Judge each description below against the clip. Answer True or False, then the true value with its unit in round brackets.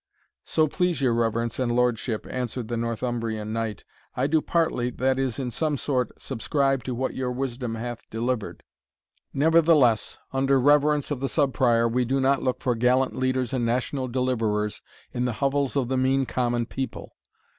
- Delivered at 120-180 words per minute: True (170 wpm)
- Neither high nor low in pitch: False (125 Hz)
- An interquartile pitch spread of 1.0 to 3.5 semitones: True (2.4 semitones)